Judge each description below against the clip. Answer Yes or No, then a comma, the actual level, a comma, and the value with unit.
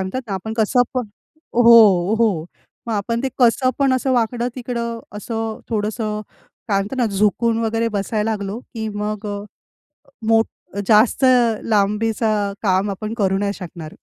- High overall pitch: Yes, high, 220 Hz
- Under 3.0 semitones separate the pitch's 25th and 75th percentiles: Yes, narrow, 2.4 semitones